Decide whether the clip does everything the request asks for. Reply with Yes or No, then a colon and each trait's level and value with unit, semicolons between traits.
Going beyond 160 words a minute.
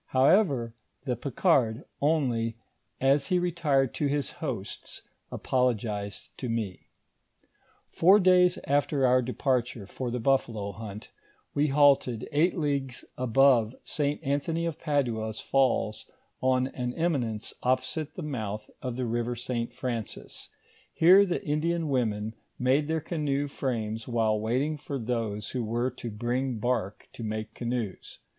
No: slow, 135 wpm